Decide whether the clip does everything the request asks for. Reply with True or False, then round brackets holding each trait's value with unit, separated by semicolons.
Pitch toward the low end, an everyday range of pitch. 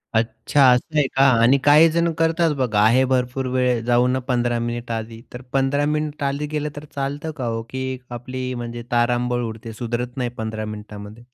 True (125 Hz; 3.0 semitones)